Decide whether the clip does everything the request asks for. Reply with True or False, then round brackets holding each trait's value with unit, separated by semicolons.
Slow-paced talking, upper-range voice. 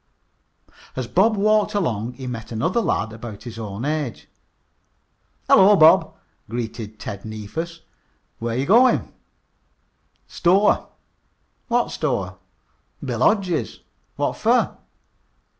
False (105 wpm; 130 Hz)